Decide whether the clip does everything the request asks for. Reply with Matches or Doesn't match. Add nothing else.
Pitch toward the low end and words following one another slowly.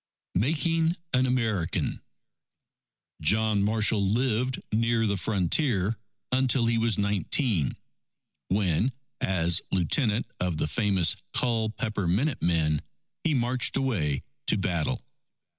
Matches